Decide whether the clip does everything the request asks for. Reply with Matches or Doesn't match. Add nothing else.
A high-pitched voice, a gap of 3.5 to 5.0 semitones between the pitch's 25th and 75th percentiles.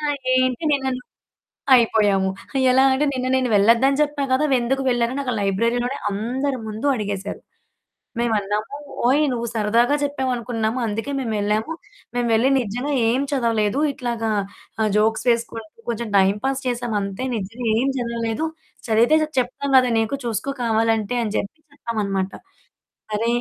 Doesn't match